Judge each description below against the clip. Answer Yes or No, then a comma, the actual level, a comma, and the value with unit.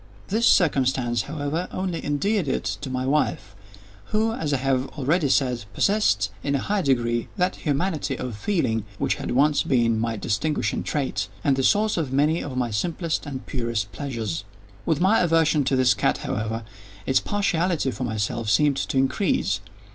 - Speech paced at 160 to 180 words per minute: Yes, average, 170 wpm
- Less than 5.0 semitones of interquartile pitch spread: No, wide, 5.5 semitones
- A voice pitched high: No, medium, 140 Hz